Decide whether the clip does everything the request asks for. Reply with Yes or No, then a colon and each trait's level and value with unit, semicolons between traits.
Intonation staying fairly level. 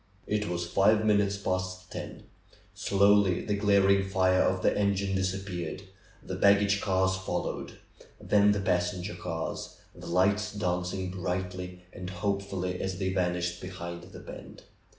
Yes: narrow, 1.7 semitones